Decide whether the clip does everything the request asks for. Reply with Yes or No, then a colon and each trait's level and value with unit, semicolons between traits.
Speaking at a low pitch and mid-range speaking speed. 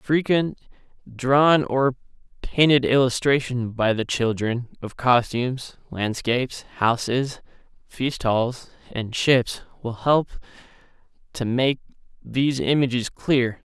No: low, 125 Hz; slow, 100 wpm